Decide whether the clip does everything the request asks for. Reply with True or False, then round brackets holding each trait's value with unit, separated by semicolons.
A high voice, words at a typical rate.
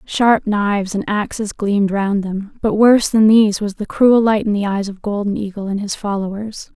False (205 Hz; 210 wpm)